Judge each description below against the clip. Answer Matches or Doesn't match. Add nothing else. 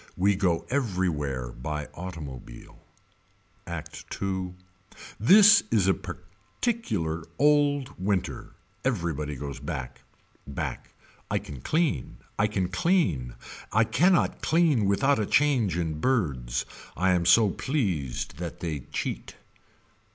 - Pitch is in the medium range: Doesn't match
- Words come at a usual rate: Doesn't match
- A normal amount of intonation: Doesn't match